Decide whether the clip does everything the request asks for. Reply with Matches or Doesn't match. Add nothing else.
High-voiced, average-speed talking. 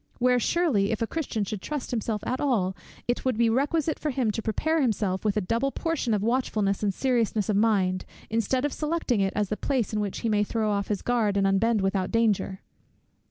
Doesn't match